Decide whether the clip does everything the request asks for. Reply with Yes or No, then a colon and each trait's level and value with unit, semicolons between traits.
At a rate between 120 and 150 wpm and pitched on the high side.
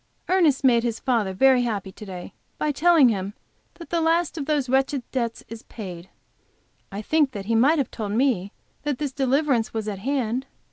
No: average, 190 wpm; very high, 250 Hz